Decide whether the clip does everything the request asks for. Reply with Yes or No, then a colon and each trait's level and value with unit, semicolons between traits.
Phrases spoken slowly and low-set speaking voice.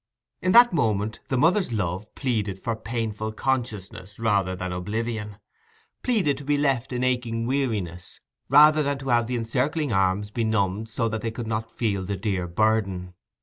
No: average, 160 wpm; low, 115 Hz